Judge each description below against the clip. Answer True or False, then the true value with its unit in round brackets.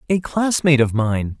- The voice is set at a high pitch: False (145 Hz)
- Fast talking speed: False (170 wpm)